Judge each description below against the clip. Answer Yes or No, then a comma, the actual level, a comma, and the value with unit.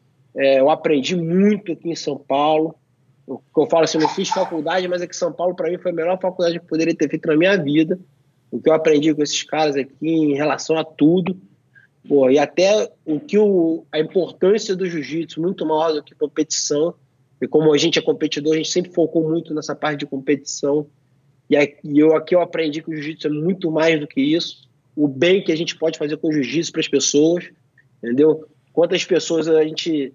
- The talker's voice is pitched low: No, medium, 155 Hz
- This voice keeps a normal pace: No, fast, 215 wpm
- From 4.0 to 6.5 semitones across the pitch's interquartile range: No, narrow, 2.4 semitones